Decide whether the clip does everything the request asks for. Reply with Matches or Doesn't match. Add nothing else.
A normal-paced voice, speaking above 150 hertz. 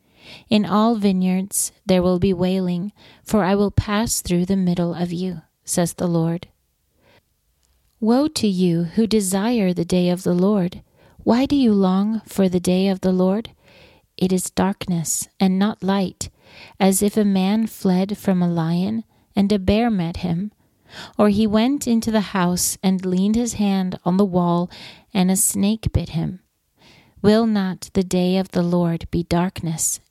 Matches